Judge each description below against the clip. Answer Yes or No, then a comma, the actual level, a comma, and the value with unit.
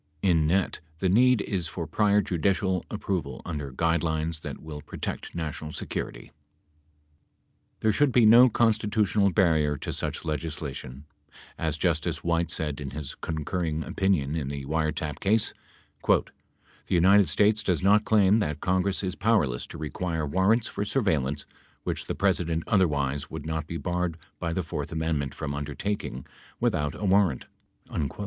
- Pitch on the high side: No, very low, 85 Hz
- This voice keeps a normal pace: Yes, average, 150 wpm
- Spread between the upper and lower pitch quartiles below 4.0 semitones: No, average, 4.6 semitones